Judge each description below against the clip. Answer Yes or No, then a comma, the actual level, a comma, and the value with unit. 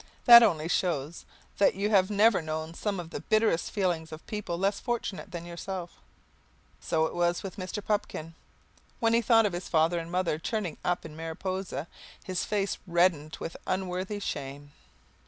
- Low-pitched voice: No, medium, 180 Hz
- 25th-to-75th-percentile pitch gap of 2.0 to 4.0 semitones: Yes, average, 3.6 semitones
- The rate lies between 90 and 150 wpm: No, average, 170 wpm